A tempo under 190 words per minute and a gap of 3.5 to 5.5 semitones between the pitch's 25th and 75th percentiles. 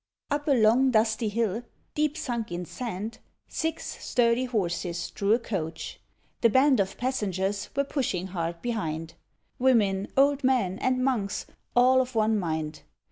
Yes: average, 145 wpm; average, 5.2 semitones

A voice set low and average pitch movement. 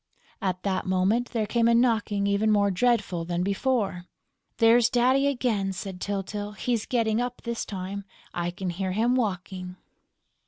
No: high, 205 Hz; average, 3.8 semitones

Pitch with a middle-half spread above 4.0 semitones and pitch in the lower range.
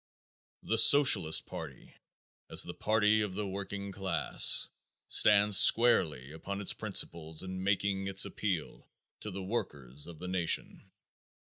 No: average, 3.4 semitones; very low, 95 Hz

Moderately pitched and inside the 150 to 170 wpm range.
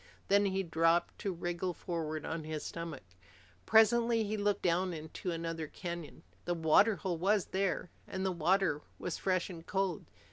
Yes: medium, 175 Hz; average, 165 wpm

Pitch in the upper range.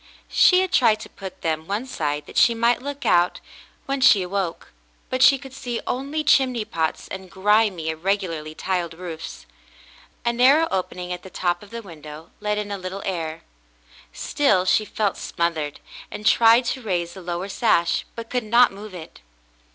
Yes: high, 195 Hz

